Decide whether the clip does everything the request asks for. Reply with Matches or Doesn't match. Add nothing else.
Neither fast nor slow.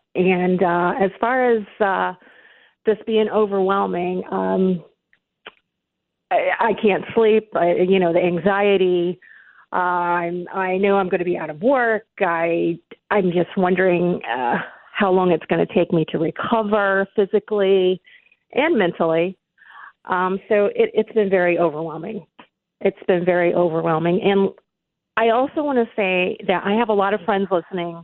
Matches